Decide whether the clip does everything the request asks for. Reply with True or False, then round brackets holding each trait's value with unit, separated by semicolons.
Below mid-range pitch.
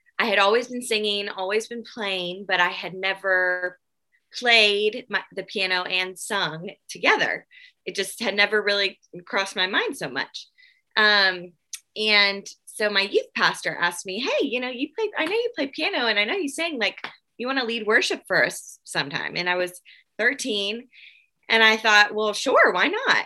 False (205 Hz)